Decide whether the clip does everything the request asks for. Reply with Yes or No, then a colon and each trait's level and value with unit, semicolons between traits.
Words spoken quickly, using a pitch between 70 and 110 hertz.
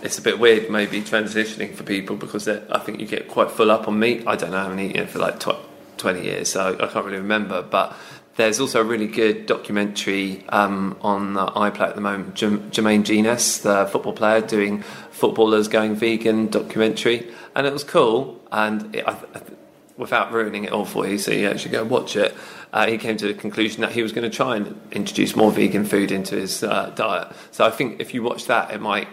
Yes: fast, 225 wpm; low, 105 Hz